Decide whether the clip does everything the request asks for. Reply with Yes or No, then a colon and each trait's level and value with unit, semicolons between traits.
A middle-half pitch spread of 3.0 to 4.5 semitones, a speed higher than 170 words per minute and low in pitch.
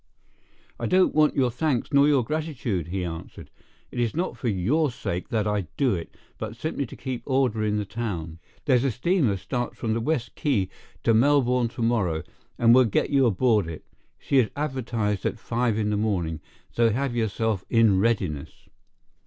Yes: average, 4.2 semitones; average, 180 wpm; low, 115 Hz